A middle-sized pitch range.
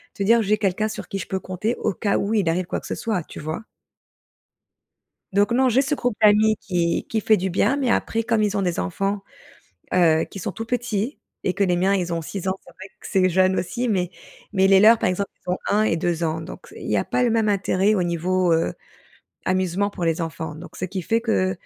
Yes: average, 3.3 semitones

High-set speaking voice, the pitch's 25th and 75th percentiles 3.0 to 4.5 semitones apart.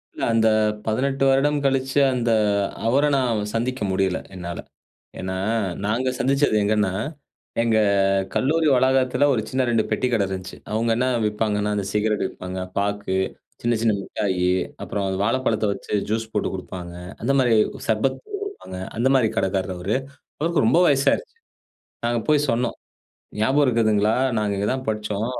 No: low, 115 Hz; average, 4.2 semitones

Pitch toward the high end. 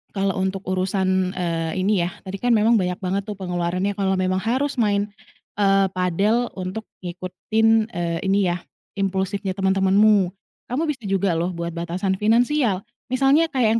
Yes: high, 195 Hz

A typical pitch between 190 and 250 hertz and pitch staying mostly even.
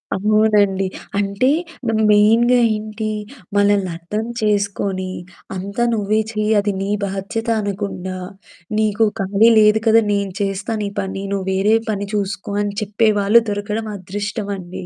Yes: high, 205 Hz; narrow, 1.5 semitones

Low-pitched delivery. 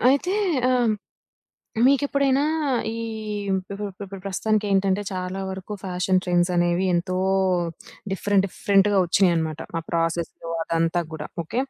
No: high, 190 Hz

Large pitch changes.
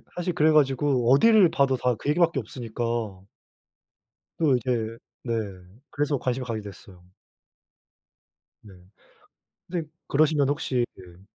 No: average, 4.5 semitones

